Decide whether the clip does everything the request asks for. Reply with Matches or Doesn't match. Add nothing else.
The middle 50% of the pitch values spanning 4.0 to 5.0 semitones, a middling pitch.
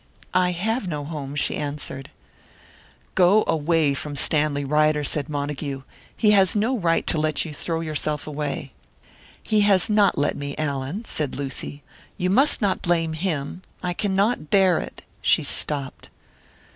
Matches